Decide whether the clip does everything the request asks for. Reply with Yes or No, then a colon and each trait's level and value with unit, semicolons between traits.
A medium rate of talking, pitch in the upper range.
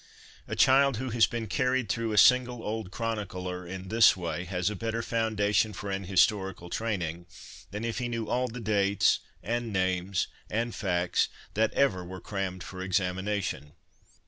No: average, 165 wpm; low, 105 Hz